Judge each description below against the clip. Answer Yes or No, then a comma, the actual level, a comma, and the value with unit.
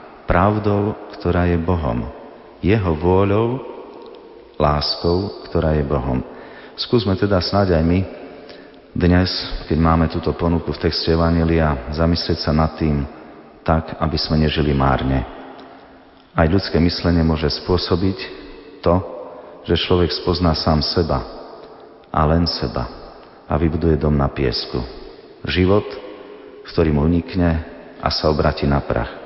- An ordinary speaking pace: Yes, average, 125 wpm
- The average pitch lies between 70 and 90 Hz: Yes, very low, 85 Hz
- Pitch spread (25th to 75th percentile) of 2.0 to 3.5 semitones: Yes, average, 2.8 semitones